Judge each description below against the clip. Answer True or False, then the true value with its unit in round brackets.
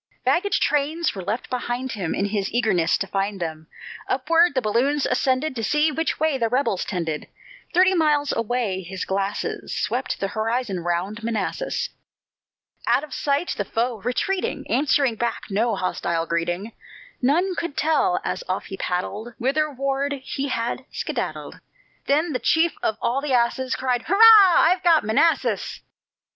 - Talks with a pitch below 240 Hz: False (250 Hz)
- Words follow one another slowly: False (155 wpm)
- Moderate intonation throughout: False (6.6 semitones)